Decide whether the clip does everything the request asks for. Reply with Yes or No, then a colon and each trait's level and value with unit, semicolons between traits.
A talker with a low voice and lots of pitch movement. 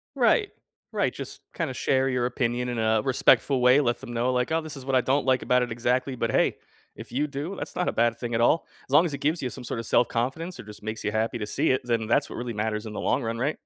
No: low, 125 Hz; average, 2.8 semitones